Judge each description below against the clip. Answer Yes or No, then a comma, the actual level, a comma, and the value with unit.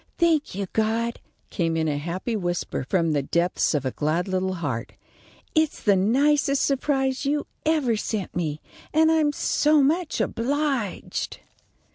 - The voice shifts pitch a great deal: Yes, wide, 9.0 semitones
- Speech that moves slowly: No, average, 145 wpm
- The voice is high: Yes, high, 220 Hz